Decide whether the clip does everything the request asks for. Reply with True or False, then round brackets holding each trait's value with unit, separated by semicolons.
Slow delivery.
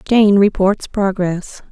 True (105 wpm)